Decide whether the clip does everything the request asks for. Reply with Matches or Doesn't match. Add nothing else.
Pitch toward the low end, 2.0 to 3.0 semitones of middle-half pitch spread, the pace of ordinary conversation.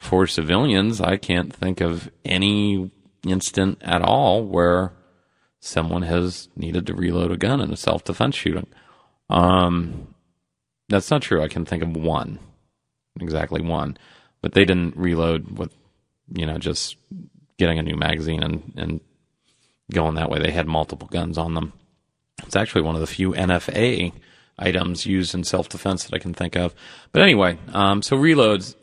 Matches